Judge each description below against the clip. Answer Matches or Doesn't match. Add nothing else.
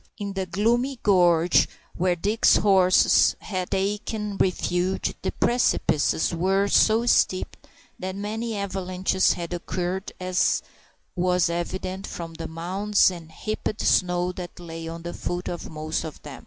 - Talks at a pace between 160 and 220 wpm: Doesn't match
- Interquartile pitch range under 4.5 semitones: Matches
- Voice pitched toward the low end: Doesn't match